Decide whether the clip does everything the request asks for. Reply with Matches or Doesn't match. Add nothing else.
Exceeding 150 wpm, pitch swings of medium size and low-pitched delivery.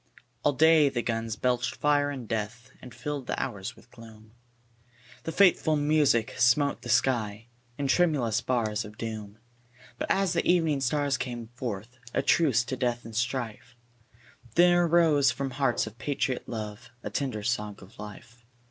Matches